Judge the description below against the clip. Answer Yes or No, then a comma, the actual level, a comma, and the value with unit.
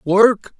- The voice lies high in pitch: Yes, high, 205 Hz